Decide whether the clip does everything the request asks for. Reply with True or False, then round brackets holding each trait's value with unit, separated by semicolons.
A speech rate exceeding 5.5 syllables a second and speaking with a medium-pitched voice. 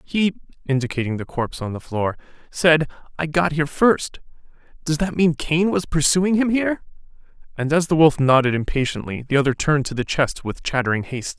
True (5.7 syllables/s; 150 Hz)